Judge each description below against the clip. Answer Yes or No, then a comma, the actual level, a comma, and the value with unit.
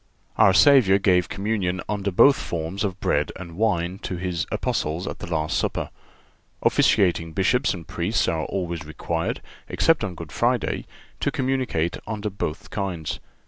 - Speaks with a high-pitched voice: No, very low, 95 Hz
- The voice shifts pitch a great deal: No, average, 3.7 semitones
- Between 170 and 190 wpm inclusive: No, average, 150 wpm